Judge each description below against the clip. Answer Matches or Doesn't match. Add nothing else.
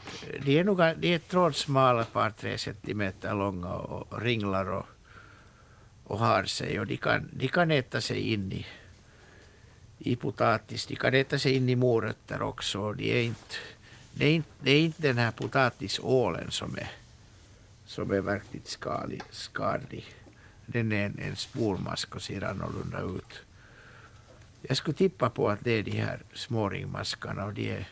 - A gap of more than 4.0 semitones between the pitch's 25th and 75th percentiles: Matches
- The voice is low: Matches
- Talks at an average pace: Matches